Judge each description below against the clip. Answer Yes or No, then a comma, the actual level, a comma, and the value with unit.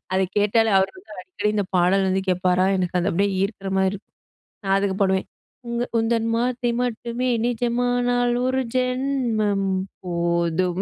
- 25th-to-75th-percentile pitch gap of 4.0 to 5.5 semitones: Yes, average, 4.3 semitones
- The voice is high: Yes, high, 205 Hz